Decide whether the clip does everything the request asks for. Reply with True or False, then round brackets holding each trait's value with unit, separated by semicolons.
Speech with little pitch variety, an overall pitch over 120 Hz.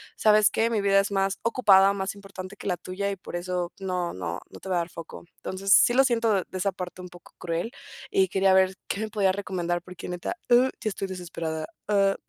True (2.1 semitones; 190 Hz)